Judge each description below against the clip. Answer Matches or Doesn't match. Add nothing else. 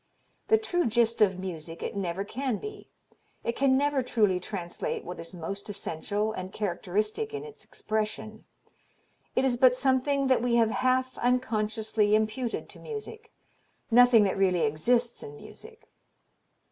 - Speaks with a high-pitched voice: Matches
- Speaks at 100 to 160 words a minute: Matches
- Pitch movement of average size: Matches